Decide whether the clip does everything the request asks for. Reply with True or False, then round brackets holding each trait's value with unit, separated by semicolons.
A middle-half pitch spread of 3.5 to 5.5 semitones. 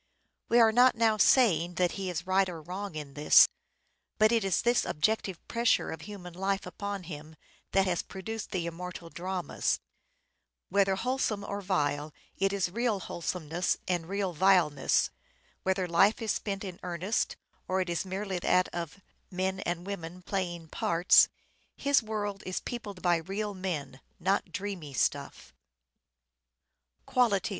False (2.7 semitones)